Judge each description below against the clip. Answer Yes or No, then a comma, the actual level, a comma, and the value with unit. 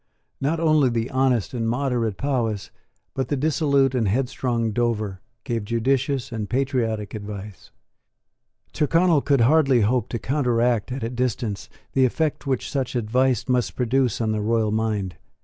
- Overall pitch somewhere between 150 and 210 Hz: No, low, 125 Hz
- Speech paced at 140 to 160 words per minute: Yes, average, 150 wpm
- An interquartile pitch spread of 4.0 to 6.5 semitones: No, average, 3.3 semitones